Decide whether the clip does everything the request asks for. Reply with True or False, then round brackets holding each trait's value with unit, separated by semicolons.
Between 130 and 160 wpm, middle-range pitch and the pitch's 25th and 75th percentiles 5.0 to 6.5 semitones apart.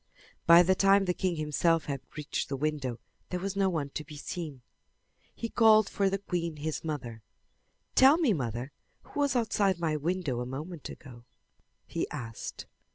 False (170 wpm; 165 Hz; 5.3 semitones)